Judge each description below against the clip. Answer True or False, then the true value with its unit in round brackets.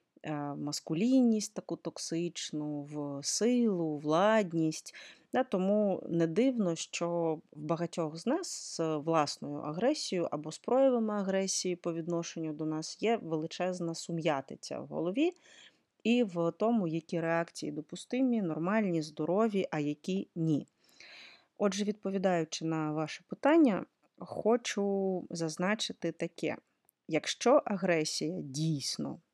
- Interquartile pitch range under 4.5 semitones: False (4.8 semitones)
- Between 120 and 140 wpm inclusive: False (110 wpm)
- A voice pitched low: False (170 Hz)